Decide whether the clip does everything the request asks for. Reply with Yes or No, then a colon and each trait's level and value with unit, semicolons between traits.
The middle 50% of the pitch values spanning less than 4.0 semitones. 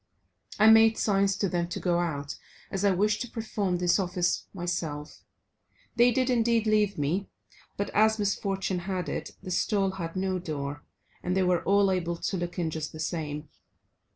Yes: average, 3.0 semitones